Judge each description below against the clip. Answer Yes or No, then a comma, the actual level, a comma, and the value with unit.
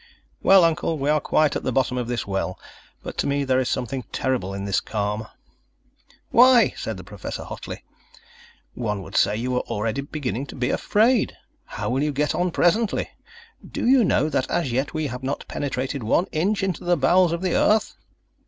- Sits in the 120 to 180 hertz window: Yes, low, 135 Hz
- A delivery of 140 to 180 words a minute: No, average, 195 wpm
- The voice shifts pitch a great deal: Yes, wide, 6.3 semitones